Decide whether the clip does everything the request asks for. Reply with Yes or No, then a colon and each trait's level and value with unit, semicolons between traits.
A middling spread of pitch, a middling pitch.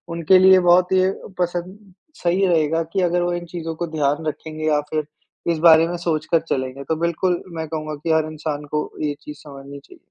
No: narrow, 2.3 semitones; medium, 165 Hz